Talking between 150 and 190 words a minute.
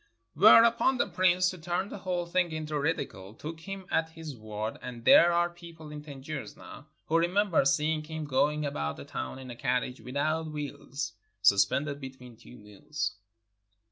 Yes: average, 170 wpm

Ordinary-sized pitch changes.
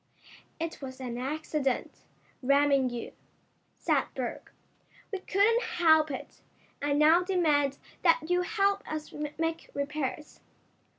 Yes: average, 4.2 semitones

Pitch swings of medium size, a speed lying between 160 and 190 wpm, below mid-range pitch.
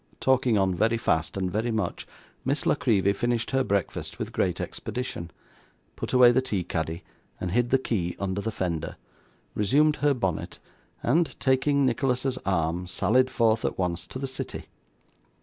No: wide, 5.8 semitones; average, 165 wpm; low, 115 Hz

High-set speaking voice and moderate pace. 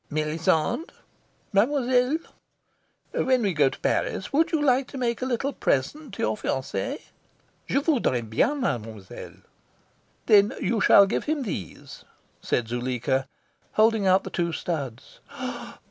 No: high, 200 Hz; slow, 130 wpm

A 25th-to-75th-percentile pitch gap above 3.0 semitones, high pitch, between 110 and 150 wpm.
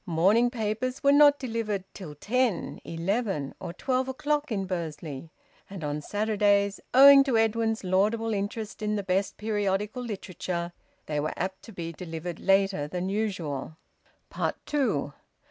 Yes: average, 4.4 semitones; high, 200 Hz; average, 140 wpm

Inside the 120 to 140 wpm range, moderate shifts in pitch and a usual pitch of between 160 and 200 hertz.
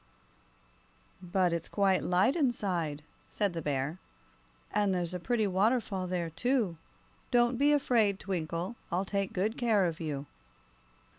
Yes: slow, 135 wpm; average, 4.7 semitones; high, 190 Hz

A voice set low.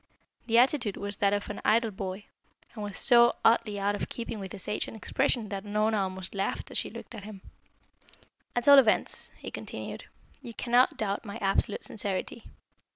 No: high, 210 Hz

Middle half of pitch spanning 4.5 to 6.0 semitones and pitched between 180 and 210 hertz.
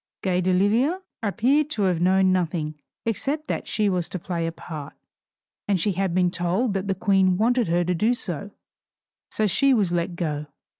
No: average, 3.8 semitones; high, 190 Hz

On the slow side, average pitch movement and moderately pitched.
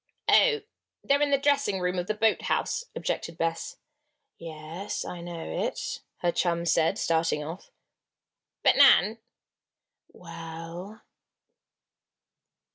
Yes: slow, 110 wpm; average, 4.5 semitones; medium, 175 Hz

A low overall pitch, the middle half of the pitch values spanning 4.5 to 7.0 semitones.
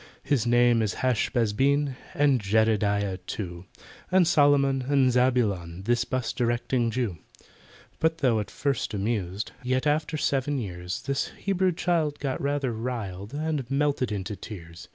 Yes: low, 125 Hz; average, 5.2 semitones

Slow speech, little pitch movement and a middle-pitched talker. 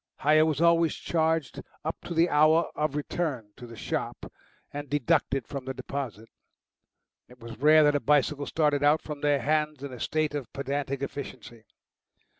No: average, 170 wpm; narrow, 2.3 semitones; medium, 145 Hz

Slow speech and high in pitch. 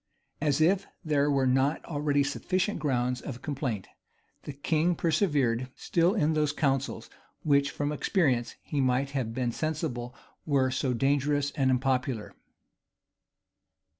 No: slow, 130 wpm; medium, 140 Hz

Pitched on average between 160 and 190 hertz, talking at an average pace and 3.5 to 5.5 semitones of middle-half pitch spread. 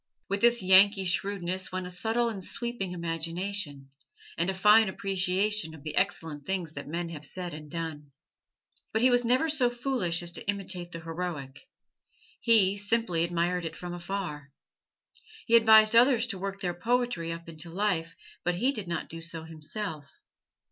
Yes: medium, 185 Hz; average, 170 wpm; average, 4.2 semitones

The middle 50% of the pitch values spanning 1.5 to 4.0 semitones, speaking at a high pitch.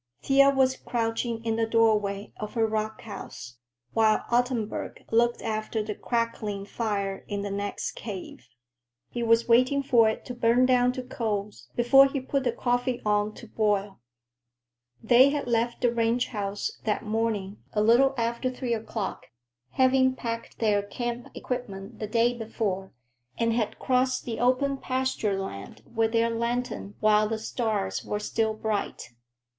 Yes: narrow, 2.6 semitones; high, 230 Hz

